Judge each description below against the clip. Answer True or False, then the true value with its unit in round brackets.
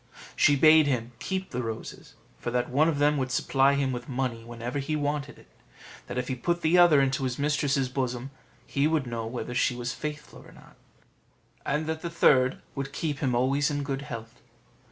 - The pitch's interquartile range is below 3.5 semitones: True (3.0 semitones)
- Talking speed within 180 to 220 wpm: True (200 wpm)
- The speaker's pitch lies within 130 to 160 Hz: True (135 Hz)